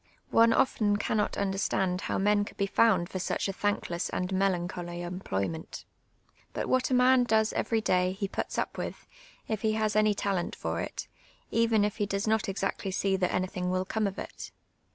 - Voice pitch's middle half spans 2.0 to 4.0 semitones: Yes, average, 2.8 semitones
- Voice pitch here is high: Yes, high, 200 Hz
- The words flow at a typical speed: Yes, average, 190 wpm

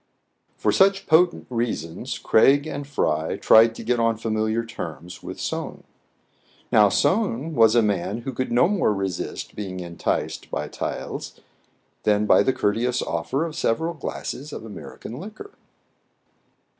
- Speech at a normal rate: Yes, average, 145 wpm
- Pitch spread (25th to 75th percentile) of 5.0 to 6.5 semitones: Yes, wide, 5.6 semitones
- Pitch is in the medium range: No, low, 115 Hz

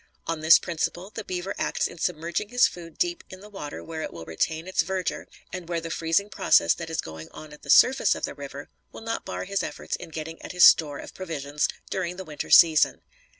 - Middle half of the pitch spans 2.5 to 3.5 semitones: Yes, average, 3.0 semitones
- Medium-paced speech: No, fast, 230 wpm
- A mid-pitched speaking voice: Yes, medium, 170 Hz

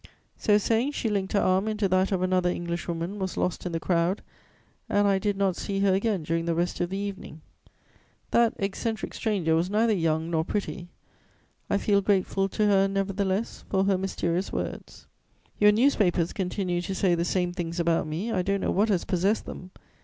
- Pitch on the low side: No, high, 190 Hz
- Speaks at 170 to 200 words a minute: Yes, average, 190 wpm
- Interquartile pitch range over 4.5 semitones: No, narrow, 2.6 semitones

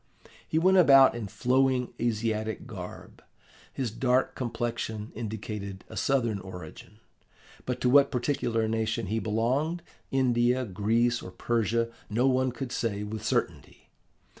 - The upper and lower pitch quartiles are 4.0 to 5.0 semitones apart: No, average, 3.1 semitones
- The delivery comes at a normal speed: No, slow, 130 wpm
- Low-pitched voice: Yes, low, 115 Hz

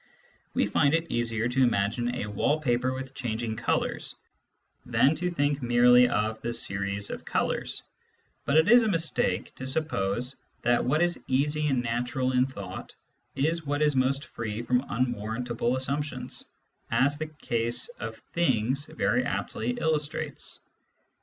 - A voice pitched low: Yes, low, 130 Hz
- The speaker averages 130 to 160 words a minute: Yes, average, 150 wpm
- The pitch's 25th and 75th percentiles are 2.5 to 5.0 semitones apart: Yes, average, 3.7 semitones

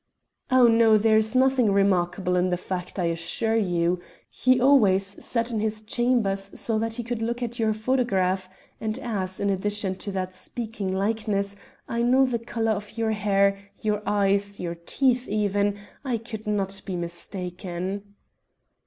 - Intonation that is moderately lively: Yes, average, 3.0 semitones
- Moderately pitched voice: No, high, 210 Hz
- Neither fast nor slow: Yes, average, 160 wpm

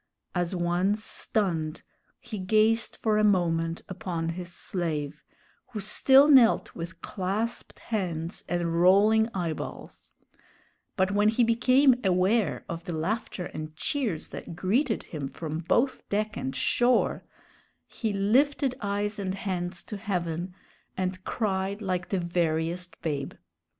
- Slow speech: Yes, slow, 130 wpm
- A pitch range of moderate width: Yes, average, 4.1 semitones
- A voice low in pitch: No, medium, 185 Hz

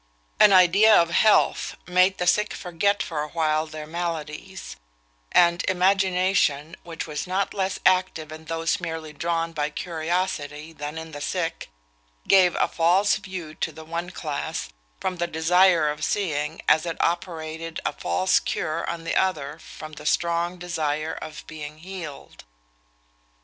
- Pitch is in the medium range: Yes, medium, 165 Hz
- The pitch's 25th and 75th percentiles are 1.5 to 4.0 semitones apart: Yes, average, 2.7 semitones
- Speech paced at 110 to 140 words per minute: No, average, 150 wpm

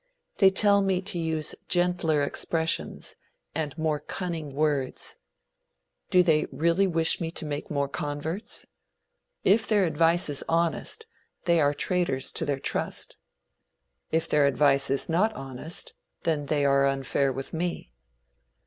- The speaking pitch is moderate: Yes, medium, 160 Hz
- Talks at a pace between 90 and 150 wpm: Yes, average, 140 wpm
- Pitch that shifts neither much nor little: Yes, average, 3.4 semitones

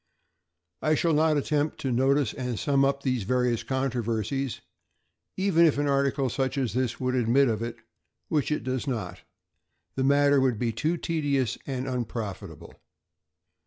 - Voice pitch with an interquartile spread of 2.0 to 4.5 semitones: Yes, average, 2.9 semitones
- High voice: No, low, 130 Hz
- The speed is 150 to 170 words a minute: Yes, average, 155 wpm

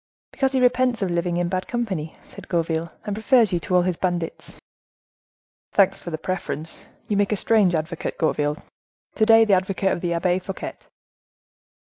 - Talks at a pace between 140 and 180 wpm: Yes, average, 175 wpm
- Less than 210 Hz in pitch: Yes, medium, 185 Hz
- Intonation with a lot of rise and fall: No, average, 3.7 semitones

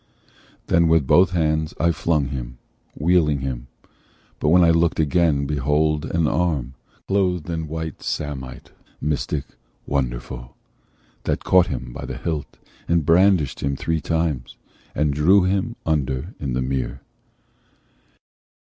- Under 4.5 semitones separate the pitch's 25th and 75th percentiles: Yes, average, 3.7 semitones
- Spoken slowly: Yes, slow, 130 wpm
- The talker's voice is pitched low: Yes, very low, 75 Hz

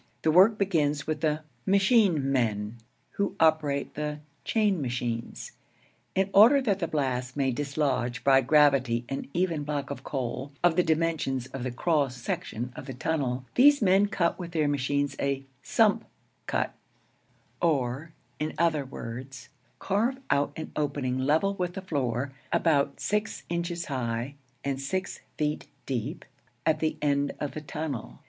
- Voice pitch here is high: No, medium, 145 Hz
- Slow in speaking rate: No, average, 150 wpm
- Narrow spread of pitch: No, average, 4.4 semitones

